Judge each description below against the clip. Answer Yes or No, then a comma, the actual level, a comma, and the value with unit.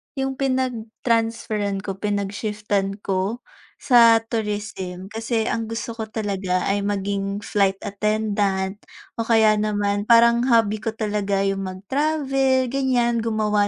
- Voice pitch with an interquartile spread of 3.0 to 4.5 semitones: No, narrow, 2.5 semitones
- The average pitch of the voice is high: Yes, high, 215 Hz